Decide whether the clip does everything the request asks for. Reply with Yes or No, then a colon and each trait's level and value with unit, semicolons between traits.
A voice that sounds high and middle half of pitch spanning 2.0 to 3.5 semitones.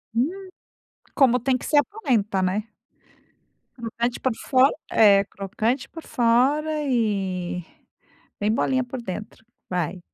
No: high, 235 Hz; average, 4.7 semitones